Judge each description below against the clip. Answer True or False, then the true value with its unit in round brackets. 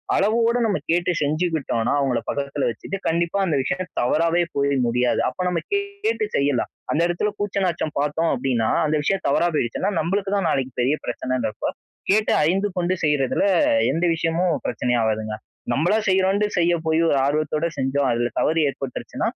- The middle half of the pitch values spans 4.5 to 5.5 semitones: True (5.2 semitones)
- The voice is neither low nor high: True (160 Hz)